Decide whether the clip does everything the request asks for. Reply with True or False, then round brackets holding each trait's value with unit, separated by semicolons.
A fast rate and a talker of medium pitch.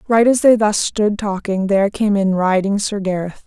False (210 wpm; 205 Hz)